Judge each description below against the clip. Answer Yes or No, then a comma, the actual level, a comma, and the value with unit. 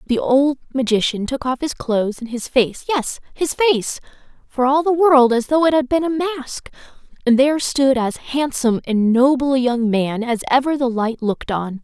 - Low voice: No, very high, 260 Hz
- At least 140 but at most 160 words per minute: No, average, 195 wpm